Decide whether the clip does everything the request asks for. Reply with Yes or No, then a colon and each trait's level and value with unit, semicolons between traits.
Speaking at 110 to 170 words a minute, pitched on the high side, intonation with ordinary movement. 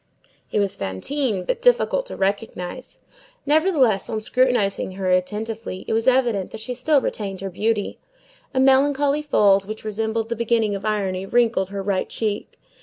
Yes: average, 160 wpm; high, 220 Hz; average, 4.6 semitones